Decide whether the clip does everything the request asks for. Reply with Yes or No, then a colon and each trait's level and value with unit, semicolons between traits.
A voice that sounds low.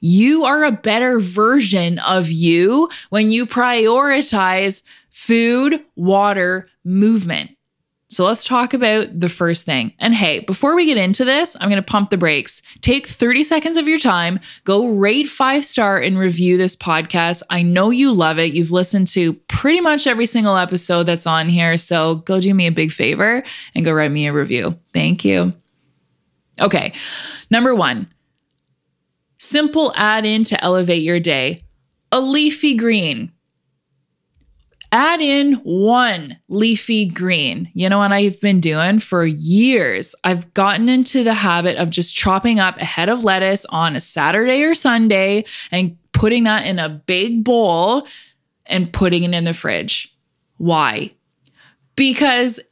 No: high, 195 Hz